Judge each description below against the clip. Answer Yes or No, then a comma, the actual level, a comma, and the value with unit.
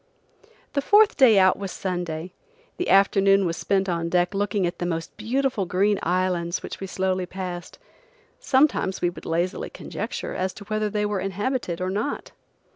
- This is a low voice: No, high, 190 Hz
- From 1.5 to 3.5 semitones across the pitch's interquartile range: Yes, average, 2.7 semitones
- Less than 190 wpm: Yes, average, 170 wpm